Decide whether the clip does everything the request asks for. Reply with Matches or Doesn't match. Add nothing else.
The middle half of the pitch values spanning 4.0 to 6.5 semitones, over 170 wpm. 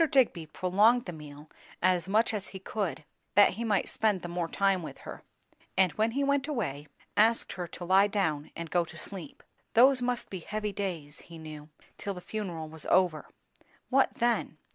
Matches